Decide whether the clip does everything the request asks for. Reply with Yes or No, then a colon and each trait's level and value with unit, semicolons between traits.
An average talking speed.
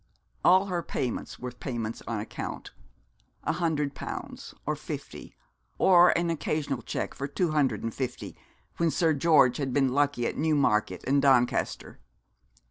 Yes: average, 145 wpm